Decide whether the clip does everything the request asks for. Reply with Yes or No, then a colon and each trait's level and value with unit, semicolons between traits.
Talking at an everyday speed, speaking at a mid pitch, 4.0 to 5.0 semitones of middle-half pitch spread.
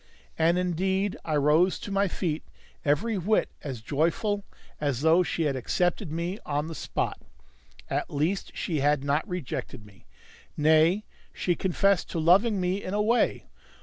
Yes: average, 155 wpm; medium, 170 Hz; average, 4.4 semitones